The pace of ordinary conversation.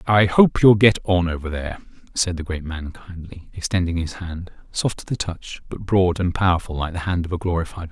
No: fast, 225 wpm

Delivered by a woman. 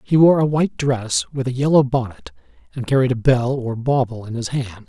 No: male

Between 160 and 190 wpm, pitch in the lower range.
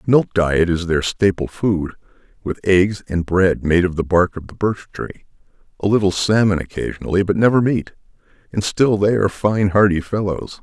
Yes: average, 180 wpm; very low, 95 Hz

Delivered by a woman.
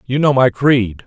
No: male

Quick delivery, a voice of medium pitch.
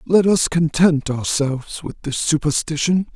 No: slow, 135 wpm; medium, 155 Hz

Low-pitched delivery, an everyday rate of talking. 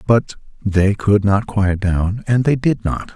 Yes: low, 105 Hz; average, 190 wpm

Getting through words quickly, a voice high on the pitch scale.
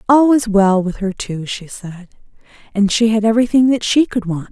Yes: fast, 215 wpm; high, 215 Hz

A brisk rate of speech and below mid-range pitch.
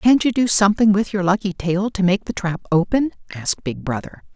No: fast, 220 wpm; high, 195 Hz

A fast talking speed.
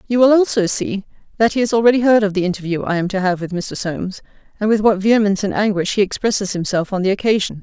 Yes: fast, 245 wpm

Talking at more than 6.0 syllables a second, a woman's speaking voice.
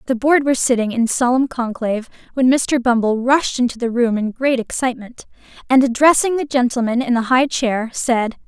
No: 5.3 syllables/s; female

